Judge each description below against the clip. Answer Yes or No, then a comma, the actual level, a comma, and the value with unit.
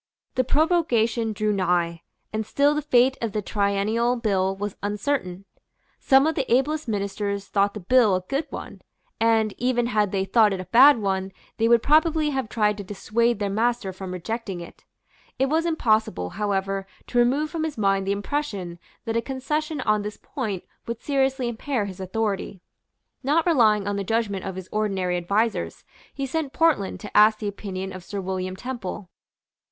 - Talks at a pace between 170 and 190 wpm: Yes, average, 180 wpm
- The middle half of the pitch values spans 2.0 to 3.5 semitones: No, average, 4.6 semitones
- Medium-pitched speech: No, high, 215 Hz